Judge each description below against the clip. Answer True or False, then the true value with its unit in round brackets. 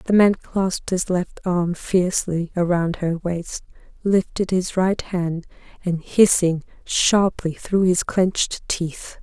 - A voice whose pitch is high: False (180 Hz)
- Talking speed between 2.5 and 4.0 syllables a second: True (3.6 syllables/s)